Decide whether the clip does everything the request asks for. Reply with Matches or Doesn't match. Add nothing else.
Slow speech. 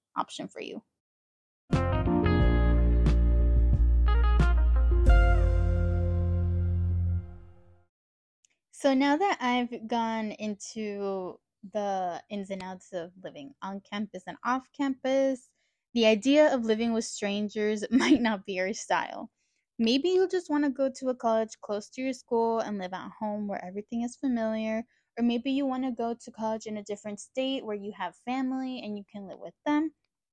Doesn't match